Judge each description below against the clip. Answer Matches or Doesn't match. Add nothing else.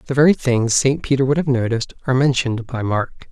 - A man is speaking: Matches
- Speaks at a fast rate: Matches